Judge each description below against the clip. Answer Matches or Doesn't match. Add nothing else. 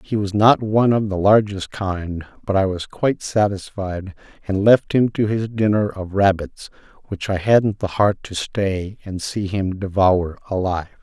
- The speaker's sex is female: Doesn't match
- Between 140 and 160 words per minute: Doesn't match